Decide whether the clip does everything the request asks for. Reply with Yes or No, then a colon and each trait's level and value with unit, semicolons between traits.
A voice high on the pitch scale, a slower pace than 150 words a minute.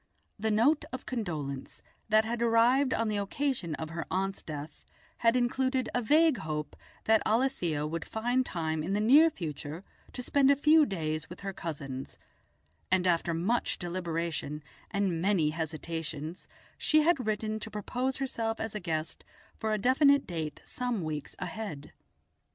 No: high, 205 Hz; average, 155 wpm